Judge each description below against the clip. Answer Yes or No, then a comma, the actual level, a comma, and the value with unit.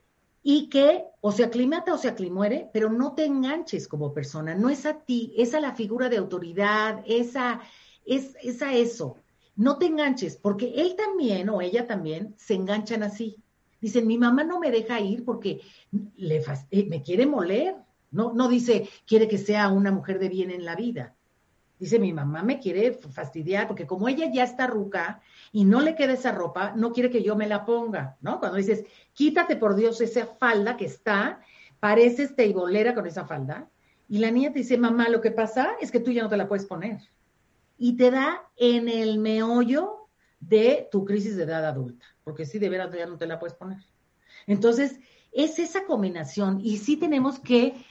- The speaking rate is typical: No, fast, 195 wpm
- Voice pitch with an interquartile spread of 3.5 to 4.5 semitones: Yes, average, 4.0 semitones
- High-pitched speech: Yes, high, 225 Hz